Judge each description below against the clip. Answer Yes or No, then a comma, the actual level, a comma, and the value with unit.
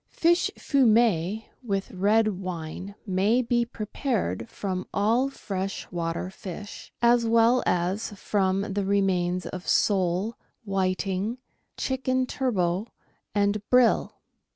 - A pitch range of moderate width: Yes, average, 3.9 semitones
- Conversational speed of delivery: No, slow, 105 wpm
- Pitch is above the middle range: Yes, high, 200 Hz